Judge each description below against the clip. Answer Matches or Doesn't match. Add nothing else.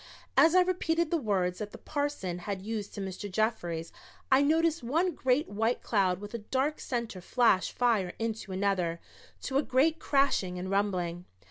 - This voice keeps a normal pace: Matches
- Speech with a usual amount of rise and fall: Doesn't match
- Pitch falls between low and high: Doesn't match